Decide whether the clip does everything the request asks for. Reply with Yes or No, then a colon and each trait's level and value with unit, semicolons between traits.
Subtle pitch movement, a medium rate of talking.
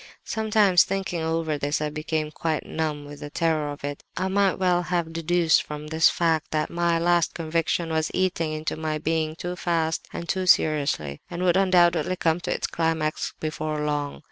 Yes: narrow, 2.2 semitones; average, 190 wpm